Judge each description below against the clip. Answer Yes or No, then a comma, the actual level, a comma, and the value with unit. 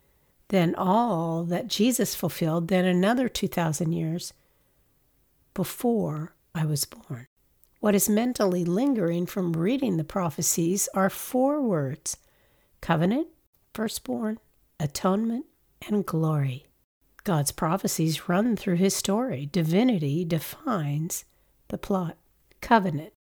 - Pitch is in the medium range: Yes, medium, 180 Hz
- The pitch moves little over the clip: No, average, 4.6 semitones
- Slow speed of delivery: Yes, slow, 105 wpm